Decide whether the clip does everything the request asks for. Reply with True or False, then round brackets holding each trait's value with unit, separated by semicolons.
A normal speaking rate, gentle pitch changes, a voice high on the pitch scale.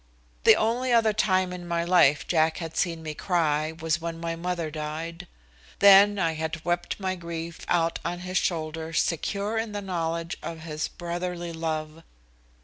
False (165 wpm; 2.1 semitones; 170 Hz)